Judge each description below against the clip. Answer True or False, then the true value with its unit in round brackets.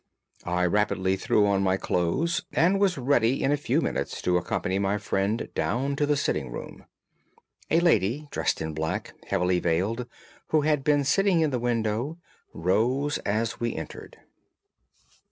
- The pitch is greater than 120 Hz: False (115 Hz)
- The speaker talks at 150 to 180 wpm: True (160 wpm)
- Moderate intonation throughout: False (7.2 semitones)